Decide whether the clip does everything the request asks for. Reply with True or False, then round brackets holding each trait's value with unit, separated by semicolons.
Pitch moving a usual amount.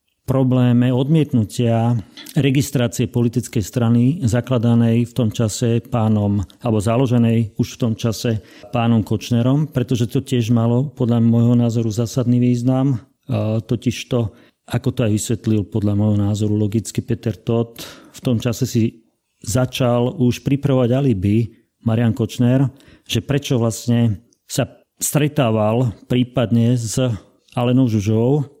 False (1.9 semitones)